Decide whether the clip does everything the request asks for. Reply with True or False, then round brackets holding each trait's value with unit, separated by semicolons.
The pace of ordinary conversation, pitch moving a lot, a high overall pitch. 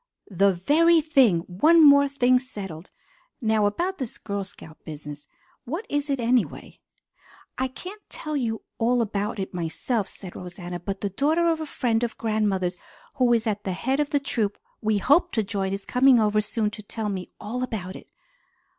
True (180 wpm; 5.7 semitones; 220 Hz)